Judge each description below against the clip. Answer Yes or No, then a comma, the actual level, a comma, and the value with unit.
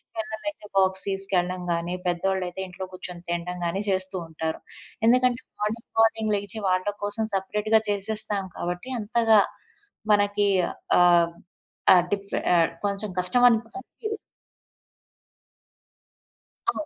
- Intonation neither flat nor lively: Yes, average, 3.3 semitones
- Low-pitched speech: No, high, 200 Hz